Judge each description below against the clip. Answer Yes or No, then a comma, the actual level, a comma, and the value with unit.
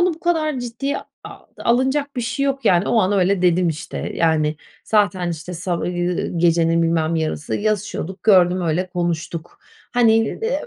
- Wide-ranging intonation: Yes, wide, 5.7 semitones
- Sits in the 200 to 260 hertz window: No, medium, 185 Hz